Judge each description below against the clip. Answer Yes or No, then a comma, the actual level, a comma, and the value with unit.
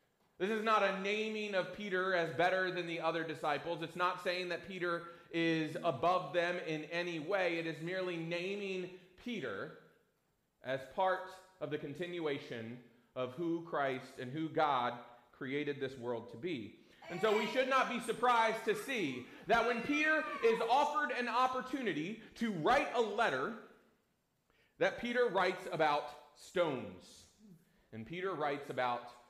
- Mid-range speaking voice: Yes, medium, 175 Hz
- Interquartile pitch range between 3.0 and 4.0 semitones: No, wide, 5.6 semitones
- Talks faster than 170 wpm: No, average, 150 wpm